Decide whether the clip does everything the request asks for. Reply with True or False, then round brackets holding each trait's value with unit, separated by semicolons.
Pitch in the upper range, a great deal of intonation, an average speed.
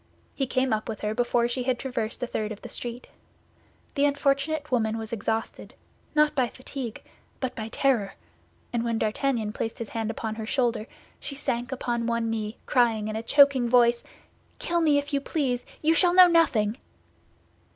False (240 Hz; 3.7 semitones; 180 wpm)